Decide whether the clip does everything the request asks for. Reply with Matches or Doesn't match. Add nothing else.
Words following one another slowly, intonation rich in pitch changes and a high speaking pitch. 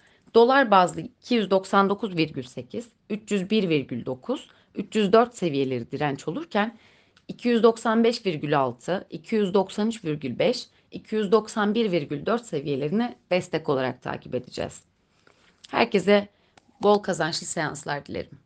Matches